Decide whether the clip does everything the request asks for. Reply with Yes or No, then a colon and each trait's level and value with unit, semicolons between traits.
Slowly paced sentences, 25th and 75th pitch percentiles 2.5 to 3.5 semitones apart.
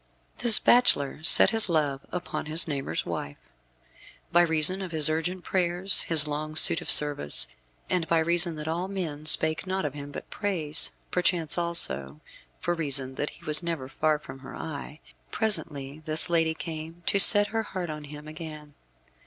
No: average, 170 wpm; average, 2.9 semitones